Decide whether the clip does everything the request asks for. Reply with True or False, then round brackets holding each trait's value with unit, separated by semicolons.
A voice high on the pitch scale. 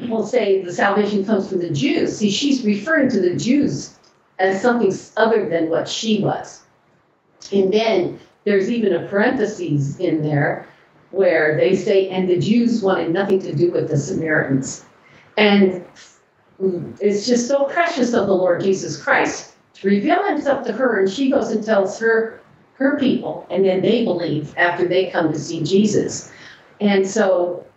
True (195 Hz)